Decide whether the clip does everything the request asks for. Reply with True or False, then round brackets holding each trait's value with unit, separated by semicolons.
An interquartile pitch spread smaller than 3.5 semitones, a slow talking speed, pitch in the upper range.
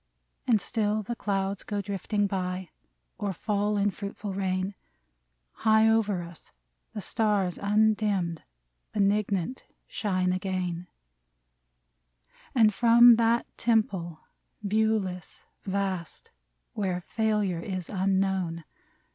True (2.5 semitones; 100 wpm; 200 Hz)